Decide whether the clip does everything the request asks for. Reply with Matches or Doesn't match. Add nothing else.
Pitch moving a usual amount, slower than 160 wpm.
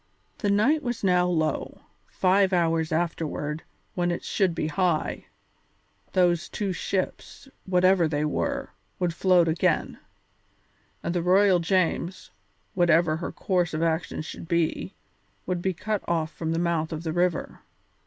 Doesn't match